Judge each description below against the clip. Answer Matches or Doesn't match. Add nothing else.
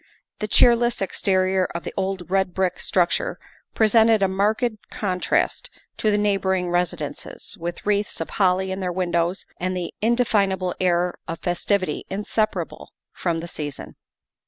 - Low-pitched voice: Doesn't match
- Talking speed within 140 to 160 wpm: Matches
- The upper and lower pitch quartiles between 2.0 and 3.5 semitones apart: Matches